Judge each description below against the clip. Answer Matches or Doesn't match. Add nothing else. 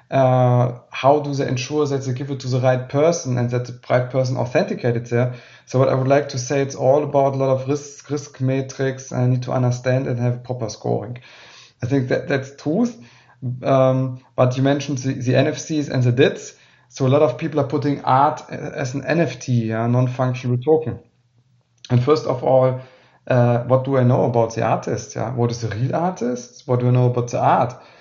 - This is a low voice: Matches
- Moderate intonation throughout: Doesn't match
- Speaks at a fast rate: Matches